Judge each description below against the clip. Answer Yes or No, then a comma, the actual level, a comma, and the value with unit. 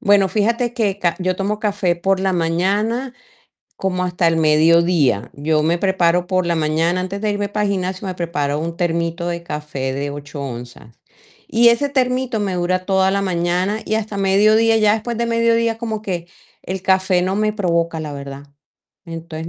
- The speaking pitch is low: No, medium, 185 Hz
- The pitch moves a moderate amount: Yes, average, 3.8 semitones